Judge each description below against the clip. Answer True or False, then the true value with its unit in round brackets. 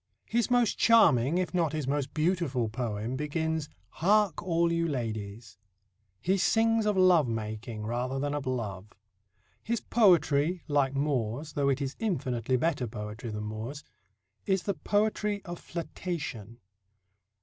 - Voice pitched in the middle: True (145 Hz)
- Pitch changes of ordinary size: False (7.1 semitones)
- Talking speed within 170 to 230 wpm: False (140 wpm)